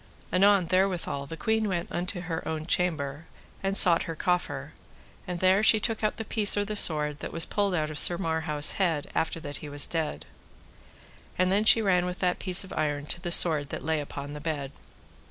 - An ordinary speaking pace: No, fast, 210 wpm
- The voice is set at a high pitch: No, medium, 170 Hz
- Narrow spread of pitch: No, average, 4.0 semitones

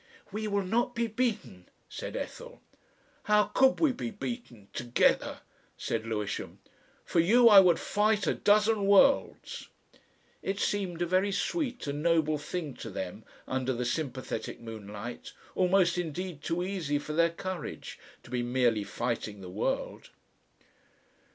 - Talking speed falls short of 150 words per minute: Yes, average, 140 wpm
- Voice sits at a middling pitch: Yes, medium, 170 Hz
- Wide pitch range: Yes, wide, 8.9 semitones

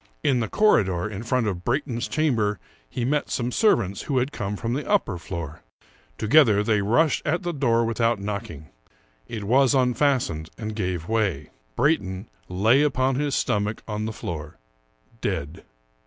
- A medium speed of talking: Yes, average, 160 wpm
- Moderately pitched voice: No, low, 115 Hz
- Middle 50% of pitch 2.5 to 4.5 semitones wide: No, average, 5.1 semitones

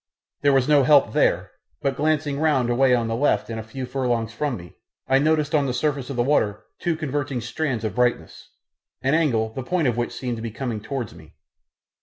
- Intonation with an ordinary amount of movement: Yes, average, 3.6 semitones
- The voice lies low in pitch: Yes, low, 130 Hz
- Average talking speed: No, fast, 215 wpm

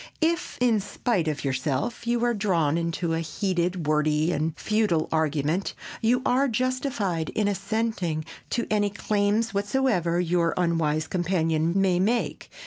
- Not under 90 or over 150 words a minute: Yes, slow, 135 wpm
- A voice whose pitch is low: No, medium, 180 Hz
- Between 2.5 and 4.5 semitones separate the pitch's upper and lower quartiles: No, average, 5.2 semitones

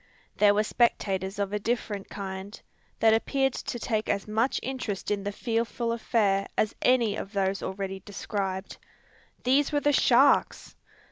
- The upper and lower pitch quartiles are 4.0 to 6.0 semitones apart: No, average, 3.0 semitones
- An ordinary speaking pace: Yes, average, 150 wpm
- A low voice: No, high, 210 Hz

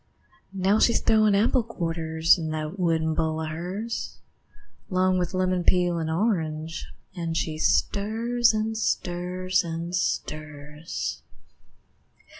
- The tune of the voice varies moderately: Yes, average, 3.7 semitones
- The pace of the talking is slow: Yes, slow, 115 wpm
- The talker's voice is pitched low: No, medium, 175 Hz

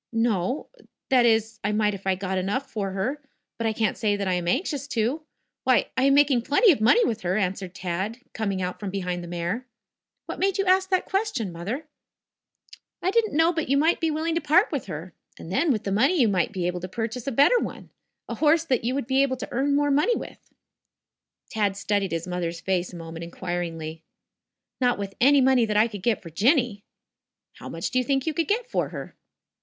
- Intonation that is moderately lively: No, wide, 7.1 semitones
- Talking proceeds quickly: Yes, fast, 225 wpm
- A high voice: Yes, high, 225 Hz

